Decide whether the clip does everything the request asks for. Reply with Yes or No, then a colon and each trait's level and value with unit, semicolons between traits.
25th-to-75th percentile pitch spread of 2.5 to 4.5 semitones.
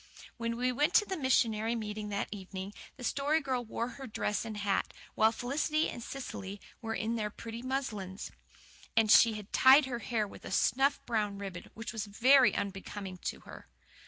Yes: average, 3.9 semitones